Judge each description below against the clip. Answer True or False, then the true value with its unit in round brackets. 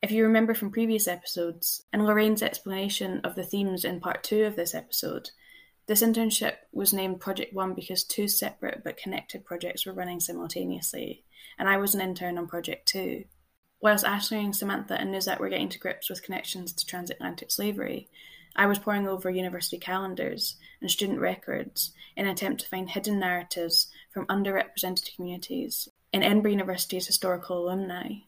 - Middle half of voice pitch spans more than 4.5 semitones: False (2.8 semitones)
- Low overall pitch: False (190 Hz)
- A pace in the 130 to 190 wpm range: True (170 wpm)